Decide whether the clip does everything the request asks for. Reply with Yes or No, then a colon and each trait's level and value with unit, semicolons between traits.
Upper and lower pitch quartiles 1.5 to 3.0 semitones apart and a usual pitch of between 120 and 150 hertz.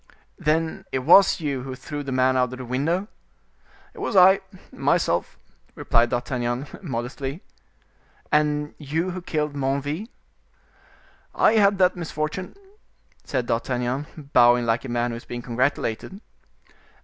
No: average, 4.5 semitones; medium, 140 Hz